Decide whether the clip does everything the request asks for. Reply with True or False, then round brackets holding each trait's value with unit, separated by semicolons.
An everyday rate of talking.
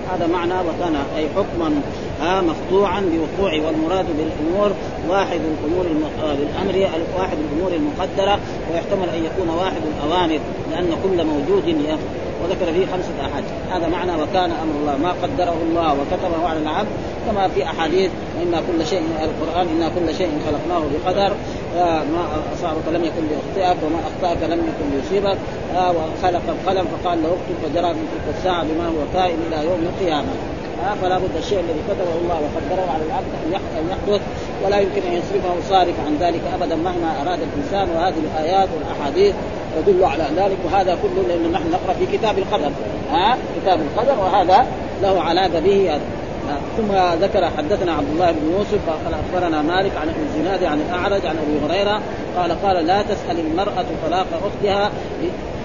False (160 wpm)